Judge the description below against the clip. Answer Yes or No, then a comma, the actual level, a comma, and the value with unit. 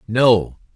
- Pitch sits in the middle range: No, low, 115 Hz